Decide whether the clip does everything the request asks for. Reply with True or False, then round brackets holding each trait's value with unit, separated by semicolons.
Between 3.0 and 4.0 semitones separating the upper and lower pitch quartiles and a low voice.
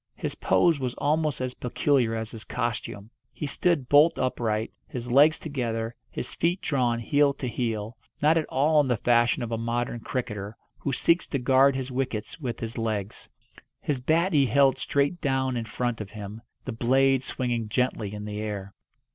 True (3.7 semitones; 125 Hz)